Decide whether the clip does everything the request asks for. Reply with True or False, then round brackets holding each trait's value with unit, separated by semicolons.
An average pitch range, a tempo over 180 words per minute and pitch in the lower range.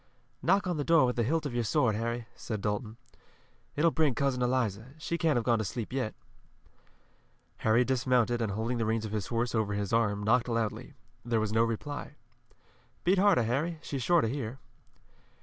True (4.0 semitones; 195 wpm; 120 Hz)